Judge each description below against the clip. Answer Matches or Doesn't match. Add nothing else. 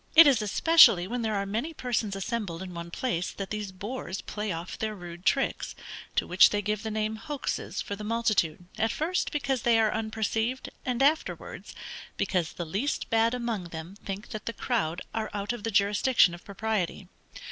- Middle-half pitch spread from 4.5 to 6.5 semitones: Doesn't match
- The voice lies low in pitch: Doesn't match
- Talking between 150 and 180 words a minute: Doesn't match